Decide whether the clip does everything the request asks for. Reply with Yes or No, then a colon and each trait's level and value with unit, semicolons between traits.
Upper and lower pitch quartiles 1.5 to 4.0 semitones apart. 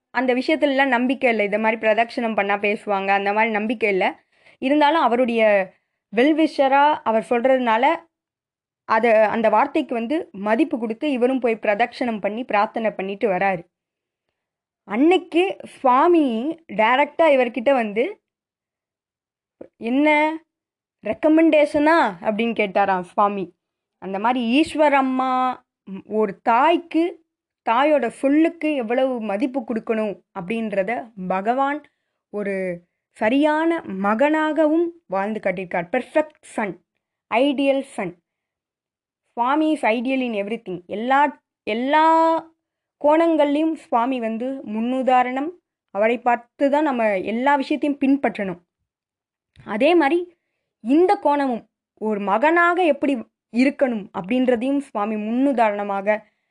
No: wide, 5.5 semitones